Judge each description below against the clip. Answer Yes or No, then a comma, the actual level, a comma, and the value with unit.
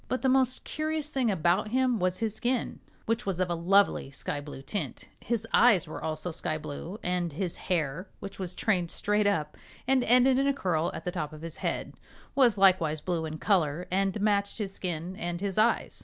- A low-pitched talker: No, high, 190 Hz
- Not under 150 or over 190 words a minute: No, fast, 205 wpm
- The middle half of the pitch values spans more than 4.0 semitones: Yes, average, 5.0 semitones